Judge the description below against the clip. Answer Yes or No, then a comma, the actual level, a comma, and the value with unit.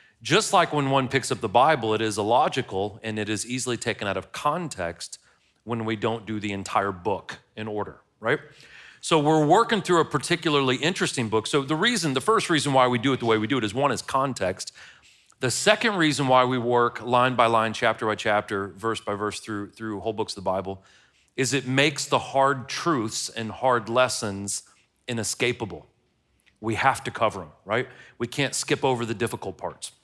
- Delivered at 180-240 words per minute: Yes, average, 200 wpm